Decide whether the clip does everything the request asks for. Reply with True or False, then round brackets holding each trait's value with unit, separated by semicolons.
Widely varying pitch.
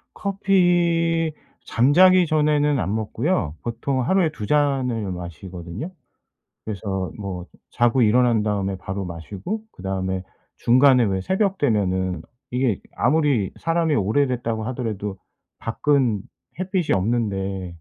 True (7.5 semitones)